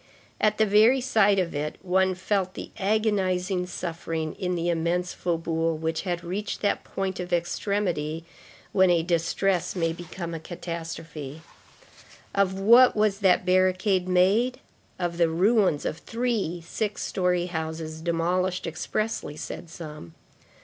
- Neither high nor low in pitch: Yes, medium, 180 Hz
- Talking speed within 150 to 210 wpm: No, slow, 135 wpm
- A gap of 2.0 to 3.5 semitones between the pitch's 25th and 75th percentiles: Yes, average, 2.9 semitones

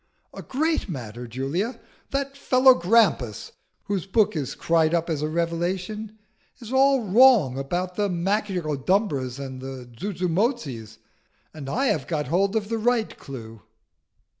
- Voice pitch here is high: No, medium, 180 Hz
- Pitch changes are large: Yes, wide, 7.9 semitones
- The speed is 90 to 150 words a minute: Yes, average, 140 wpm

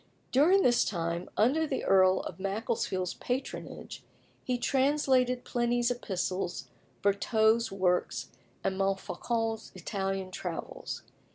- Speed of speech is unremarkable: No, slow, 100 wpm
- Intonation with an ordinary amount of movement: Yes, average, 4.6 semitones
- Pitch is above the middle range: Yes, high, 220 Hz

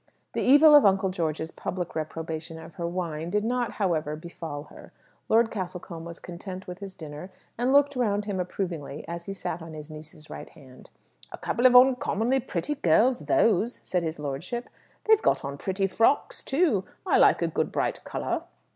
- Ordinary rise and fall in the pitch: No, wide, 6.1 semitones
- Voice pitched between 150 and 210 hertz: Yes, medium, 185 Hz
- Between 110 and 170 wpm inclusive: No, average, 180 wpm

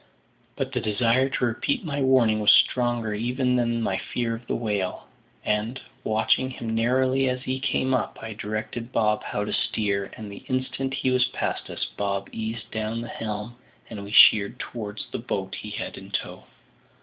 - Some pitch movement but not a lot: Yes, average, 3.1 semitones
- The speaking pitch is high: No, low, 115 Hz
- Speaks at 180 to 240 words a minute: Yes, average, 185 wpm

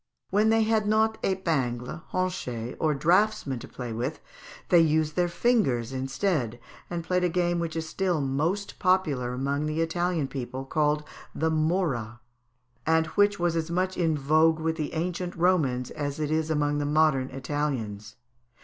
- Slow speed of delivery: No, average, 160 wpm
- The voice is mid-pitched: Yes, medium, 155 Hz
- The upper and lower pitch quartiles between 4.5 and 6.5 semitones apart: Yes, average, 4.8 semitones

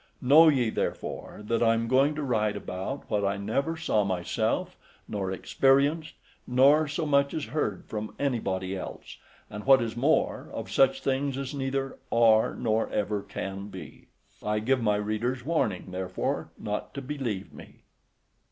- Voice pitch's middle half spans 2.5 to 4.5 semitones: No, average, 4.9 semitones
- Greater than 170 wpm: No, average, 160 wpm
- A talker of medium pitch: No, low, 120 Hz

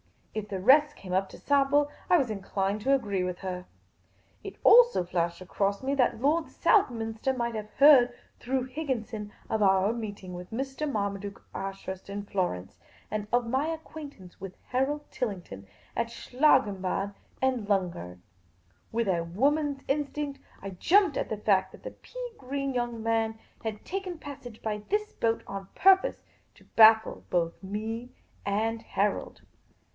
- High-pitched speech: Yes, high, 225 Hz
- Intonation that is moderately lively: No, wide, 5.8 semitones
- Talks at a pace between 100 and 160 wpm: Yes, average, 155 wpm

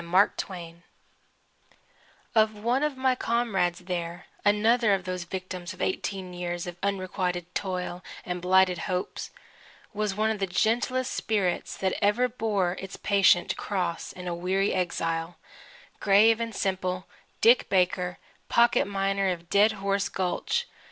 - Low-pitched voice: No, high, 190 Hz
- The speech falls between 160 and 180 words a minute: No, average, 140 wpm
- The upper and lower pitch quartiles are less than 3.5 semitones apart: Yes, average, 2.9 semitones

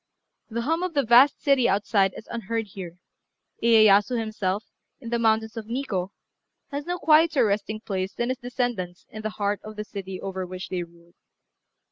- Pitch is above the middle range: Yes, high, 215 Hz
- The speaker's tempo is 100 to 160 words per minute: No, average, 175 wpm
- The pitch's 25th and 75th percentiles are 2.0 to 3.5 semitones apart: No, average, 4.0 semitones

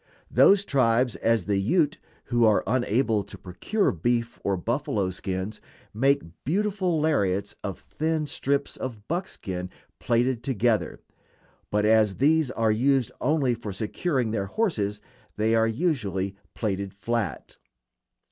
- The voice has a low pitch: Yes, low, 115 Hz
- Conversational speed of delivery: No, slow, 130 wpm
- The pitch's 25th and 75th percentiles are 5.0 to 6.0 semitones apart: Yes, wide, 5.6 semitones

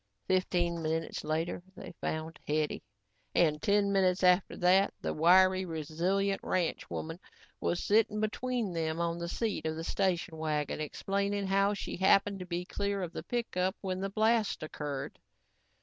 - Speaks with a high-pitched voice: No, medium, 180 Hz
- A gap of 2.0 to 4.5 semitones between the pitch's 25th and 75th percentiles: Yes, average, 3.5 semitones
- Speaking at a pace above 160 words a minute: No, average, 150 wpm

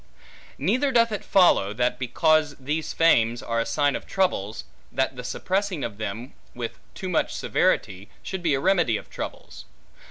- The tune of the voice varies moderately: No, wide, 8.0 semitones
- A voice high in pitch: No, medium, 140 Hz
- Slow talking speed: No, average, 165 wpm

